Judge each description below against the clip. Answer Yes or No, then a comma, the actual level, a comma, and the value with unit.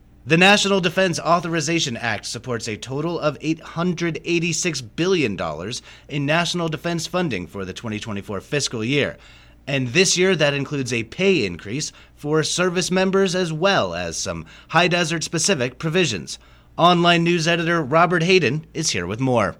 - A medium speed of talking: Yes, average, 145 wpm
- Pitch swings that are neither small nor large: No, wide, 6.4 semitones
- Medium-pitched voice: Yes, medium, 160 Hz